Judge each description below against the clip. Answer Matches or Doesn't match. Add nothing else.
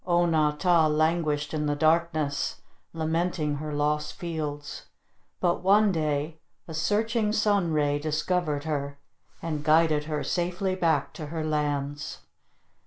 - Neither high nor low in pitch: Matches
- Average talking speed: Doesn't match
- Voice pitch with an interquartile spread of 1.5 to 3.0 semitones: Matches